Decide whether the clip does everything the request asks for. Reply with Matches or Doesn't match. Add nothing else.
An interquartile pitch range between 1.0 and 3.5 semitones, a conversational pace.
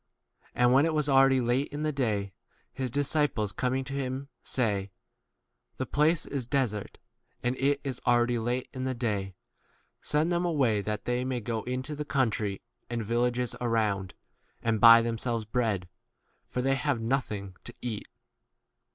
Matches